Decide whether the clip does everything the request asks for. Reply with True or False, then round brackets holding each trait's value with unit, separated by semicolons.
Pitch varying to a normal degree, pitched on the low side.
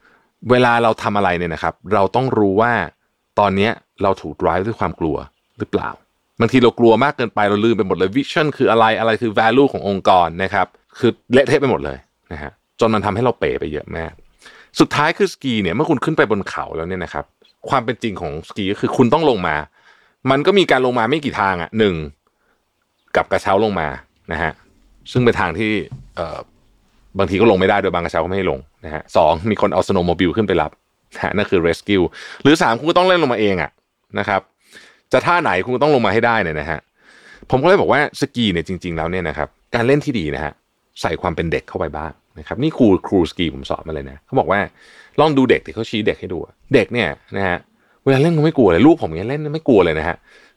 False (6.2 semitones; 105 Hz)